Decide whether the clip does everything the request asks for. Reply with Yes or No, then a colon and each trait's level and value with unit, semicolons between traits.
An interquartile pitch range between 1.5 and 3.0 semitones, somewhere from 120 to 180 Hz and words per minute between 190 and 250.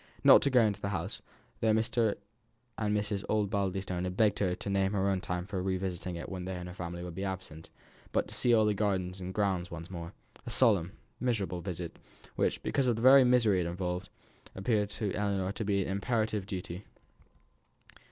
No: narrow, 2.6 semitones; very low, 95 Hz; average, 200 wpm